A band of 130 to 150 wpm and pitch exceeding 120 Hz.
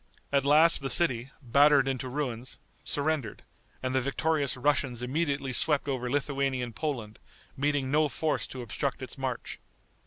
Yes: average, 145 wpm; medium, 140 Hz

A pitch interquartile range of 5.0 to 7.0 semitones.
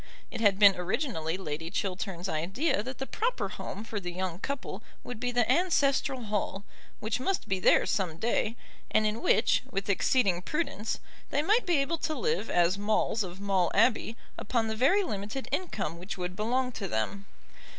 Yes: wide, 5.6 semitones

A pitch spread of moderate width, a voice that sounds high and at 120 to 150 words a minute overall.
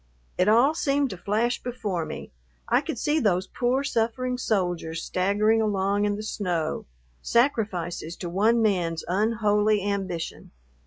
Yes: average, 4.3 semitones; high, 205 Hz; average, 140 wpm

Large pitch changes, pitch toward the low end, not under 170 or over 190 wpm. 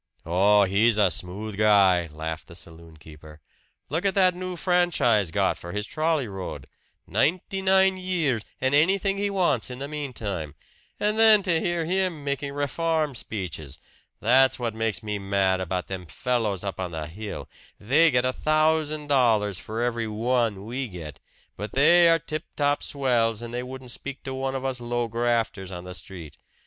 Yes: wide, 7.7 semitones; low, 120 Hz; average, 175 wpm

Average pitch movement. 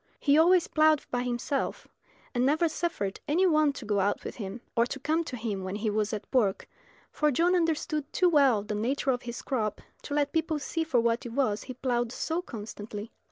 No: wide, 5.8 semitones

